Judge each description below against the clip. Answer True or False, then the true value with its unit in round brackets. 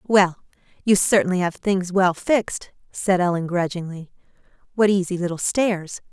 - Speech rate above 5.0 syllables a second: False (4.8 syllables/s)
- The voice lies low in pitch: False (185 Hz)